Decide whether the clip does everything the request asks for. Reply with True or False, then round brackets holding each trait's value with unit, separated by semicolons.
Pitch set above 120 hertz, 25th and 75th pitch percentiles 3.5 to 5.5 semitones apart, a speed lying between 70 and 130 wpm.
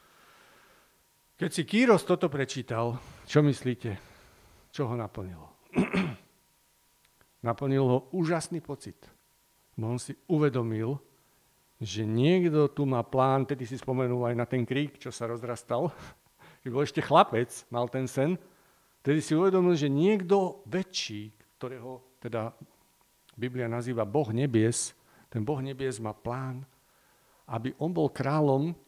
True (130 Hz; 4.2 semitones; 125 wpm)